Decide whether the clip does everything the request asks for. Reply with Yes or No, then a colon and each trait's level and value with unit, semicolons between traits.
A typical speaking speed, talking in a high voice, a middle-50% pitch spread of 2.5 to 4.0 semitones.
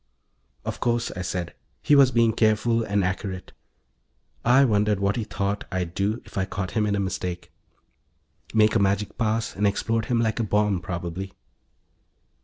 No: average, 170 wpm; low, 105 Hz; average, 2.9 semitones